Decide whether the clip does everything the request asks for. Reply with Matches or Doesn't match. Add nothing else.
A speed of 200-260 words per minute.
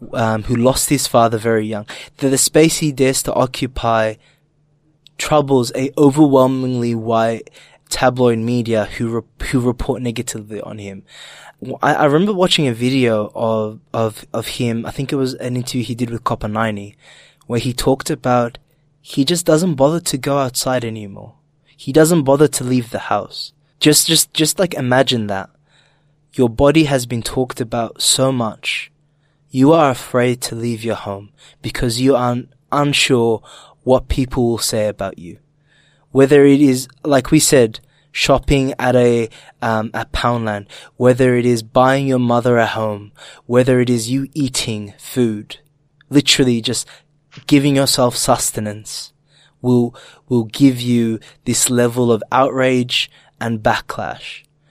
Doesn't match